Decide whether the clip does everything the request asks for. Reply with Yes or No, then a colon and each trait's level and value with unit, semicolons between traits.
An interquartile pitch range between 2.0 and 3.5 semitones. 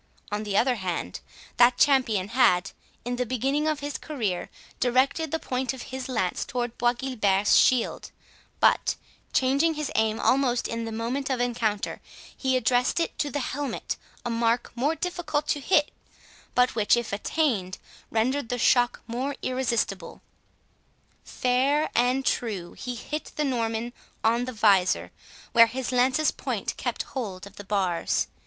Yes: average, 3.1 semitones